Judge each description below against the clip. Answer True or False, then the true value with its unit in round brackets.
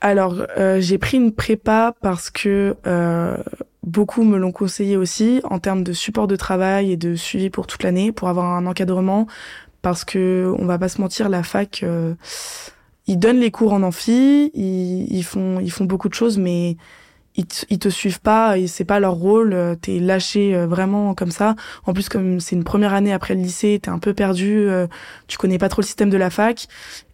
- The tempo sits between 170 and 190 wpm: False (215 wpm)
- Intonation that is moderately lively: False (2.2 semitones)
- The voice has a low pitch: False (195 Hz)